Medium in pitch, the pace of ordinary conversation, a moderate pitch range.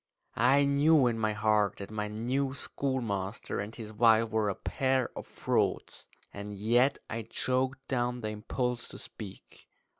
No: low, 115 Hz; average, 155 wpm; average, 3.6 semitones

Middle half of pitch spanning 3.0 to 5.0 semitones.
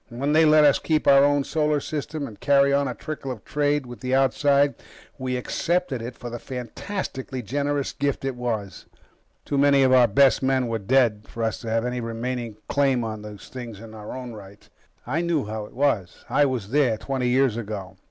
Yes: average, 3.7 semitones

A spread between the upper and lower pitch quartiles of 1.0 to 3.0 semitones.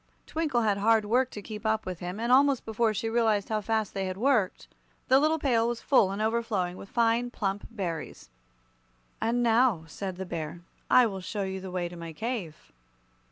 No: average, 3.8 semitones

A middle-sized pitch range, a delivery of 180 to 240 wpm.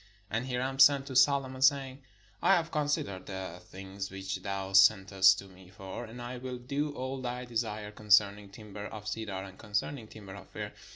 Yes: average, 5.0 semitones; average, 195 wpm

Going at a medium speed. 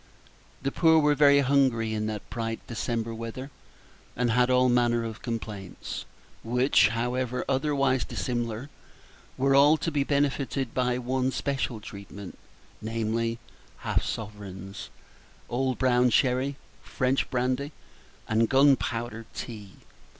No: slow, 120 wpm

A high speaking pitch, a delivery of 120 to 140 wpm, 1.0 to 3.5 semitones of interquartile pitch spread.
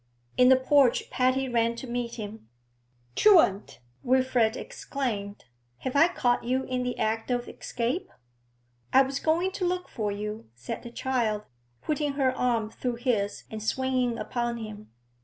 No: high, 245 Hz; average, 155 wpm; average, 2.9 semitones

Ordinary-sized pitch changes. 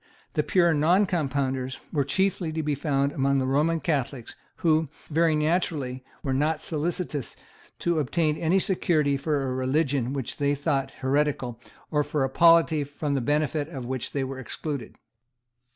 Yes: average, 3.0 semitones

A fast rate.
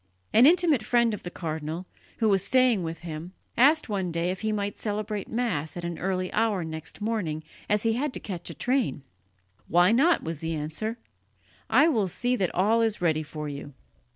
No: average, 195 wpm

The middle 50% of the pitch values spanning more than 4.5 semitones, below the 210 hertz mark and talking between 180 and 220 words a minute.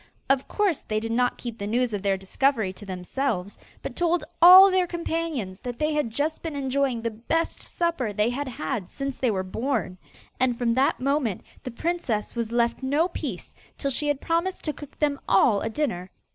No: wide, 5.4 semitones; very high, 255 Hz; average, 200 wpm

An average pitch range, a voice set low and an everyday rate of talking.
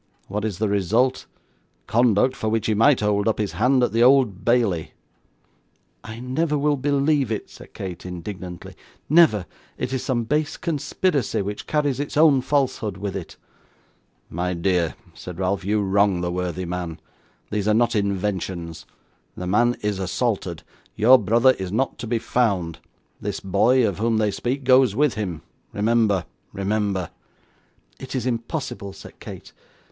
Yes: average, 4.9 semitones; low, 110 Hz; average, 155 wpm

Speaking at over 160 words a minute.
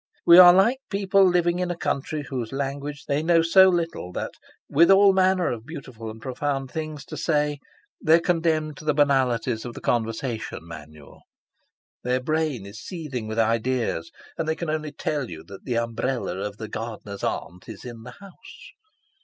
Yes: average, 180 wpm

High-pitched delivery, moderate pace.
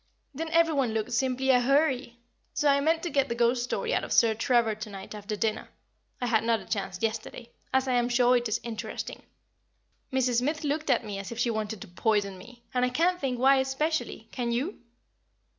No: high, 245 Hz; fast, 210 wpm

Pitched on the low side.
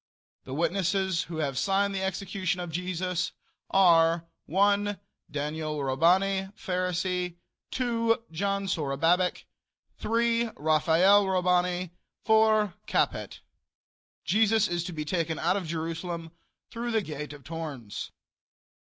No: medium, 180 Hz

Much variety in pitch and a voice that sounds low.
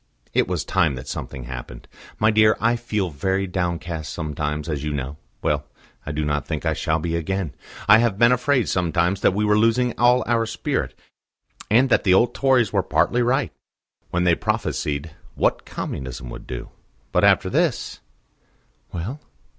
Yes: wide, 7.1 semitones; very low, 90 Hz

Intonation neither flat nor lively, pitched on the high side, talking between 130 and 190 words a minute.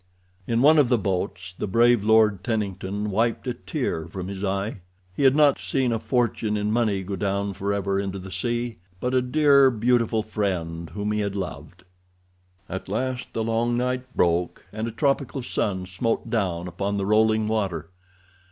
No: average, 3.9 semitones; low, 105 Hz; average, 170 wpm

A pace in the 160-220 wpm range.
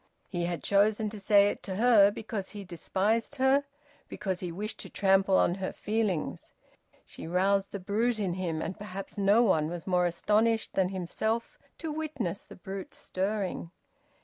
Yes: average, 170 wpm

